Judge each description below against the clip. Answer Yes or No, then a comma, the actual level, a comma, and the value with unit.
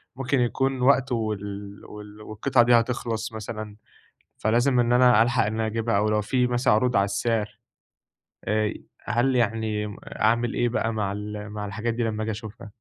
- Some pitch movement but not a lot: No, narrow, 2.3 semitones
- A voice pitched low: Yes, low, 110 Hz